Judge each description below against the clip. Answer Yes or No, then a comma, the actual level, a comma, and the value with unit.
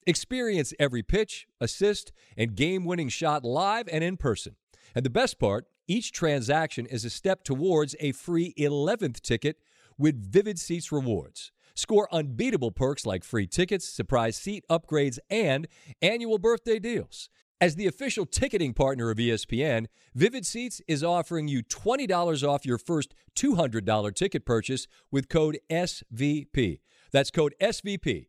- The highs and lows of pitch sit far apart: Yes, wide, 6.5 semitones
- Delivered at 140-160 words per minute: Yes, average, 145 wpm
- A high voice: No, medium, 150 Hz